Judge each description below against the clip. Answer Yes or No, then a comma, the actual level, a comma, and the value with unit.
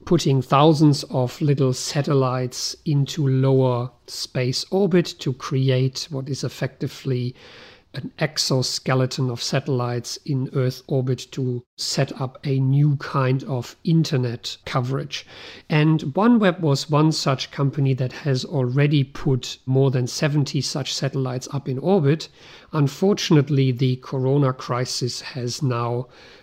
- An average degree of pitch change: No, narrow, 2.1 semitones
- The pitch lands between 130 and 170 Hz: Yes, low, 135 Hz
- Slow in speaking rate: Yes, slow, 125 wpm